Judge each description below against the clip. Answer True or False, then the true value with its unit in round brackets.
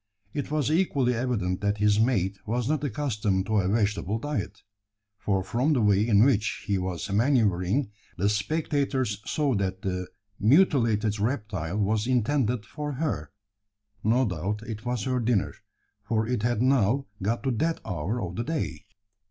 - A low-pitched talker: True (110 Hz)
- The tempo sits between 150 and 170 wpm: True (160 wpm)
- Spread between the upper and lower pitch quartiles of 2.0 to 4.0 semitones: False (4.5 semitones)